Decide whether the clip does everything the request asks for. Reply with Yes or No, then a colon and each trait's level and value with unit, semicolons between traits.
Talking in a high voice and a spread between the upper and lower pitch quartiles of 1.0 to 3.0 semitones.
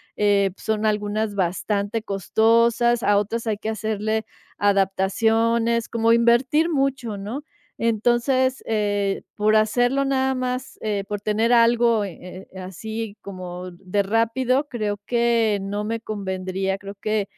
Yes: high, 220 Hz; average, 2.7 semitones